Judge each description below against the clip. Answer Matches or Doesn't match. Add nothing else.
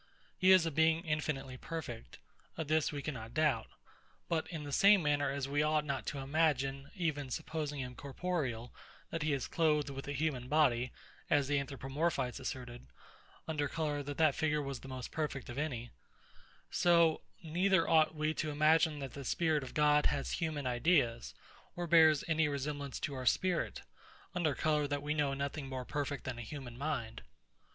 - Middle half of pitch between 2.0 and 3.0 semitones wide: Matches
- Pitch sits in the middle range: Matches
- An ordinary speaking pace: Matches